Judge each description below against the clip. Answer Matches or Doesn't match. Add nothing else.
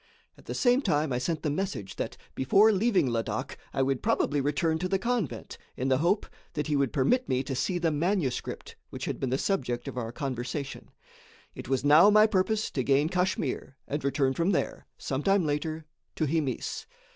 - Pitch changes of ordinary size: Doesn't match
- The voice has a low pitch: Doesn't match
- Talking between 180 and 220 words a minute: Matches